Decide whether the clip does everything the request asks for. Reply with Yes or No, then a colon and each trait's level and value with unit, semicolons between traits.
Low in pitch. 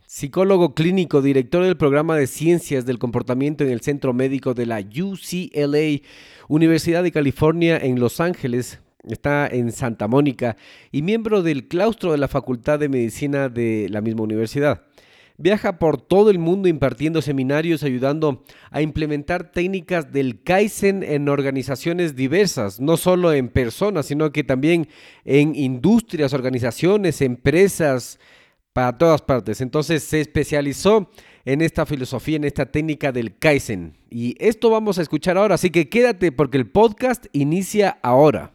No: medium, 150 Hz